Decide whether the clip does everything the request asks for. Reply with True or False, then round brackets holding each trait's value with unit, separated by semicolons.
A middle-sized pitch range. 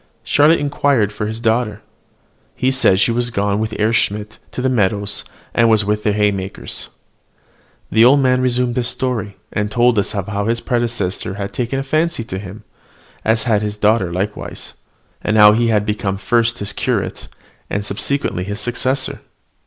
True (3.1 semitones)